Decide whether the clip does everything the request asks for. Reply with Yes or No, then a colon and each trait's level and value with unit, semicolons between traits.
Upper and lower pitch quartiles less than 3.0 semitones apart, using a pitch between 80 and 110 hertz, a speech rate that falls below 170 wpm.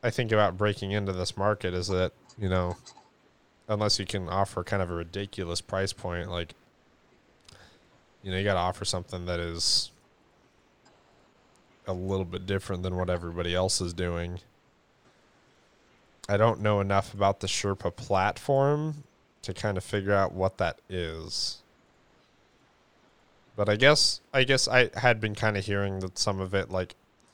Yes: narrow, 2.4 semitones; low, 100 Hz; average, 160 wpm